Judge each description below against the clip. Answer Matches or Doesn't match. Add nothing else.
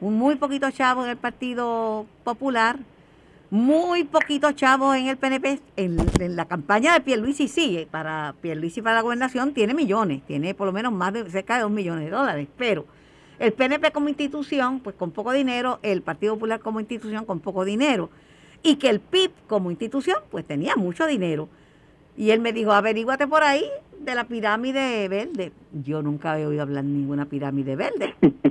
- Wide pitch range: Matches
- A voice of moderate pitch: Doesn't match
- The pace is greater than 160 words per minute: Matches